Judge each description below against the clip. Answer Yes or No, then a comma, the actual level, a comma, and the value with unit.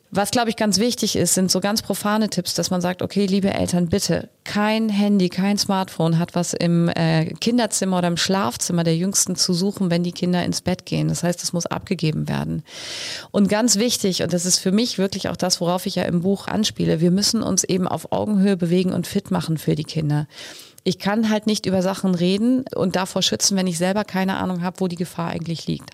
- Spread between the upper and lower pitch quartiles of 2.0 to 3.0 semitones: Yes, narrow, 2.5 semitones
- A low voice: No, medium, 185 Hz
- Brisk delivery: Yes, fast, 225 wpm